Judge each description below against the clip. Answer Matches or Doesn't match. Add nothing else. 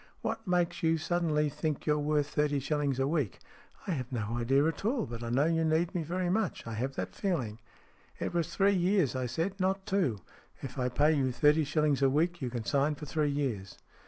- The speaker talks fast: Matches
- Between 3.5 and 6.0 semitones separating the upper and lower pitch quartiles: Matches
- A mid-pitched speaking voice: Matches